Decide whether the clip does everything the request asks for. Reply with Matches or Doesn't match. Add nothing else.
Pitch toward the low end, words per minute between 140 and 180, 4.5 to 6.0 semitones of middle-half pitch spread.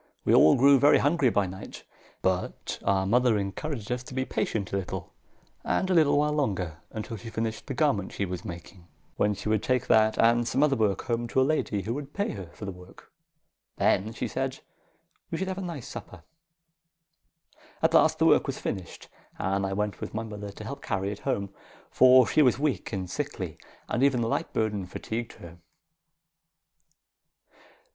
Doesn't match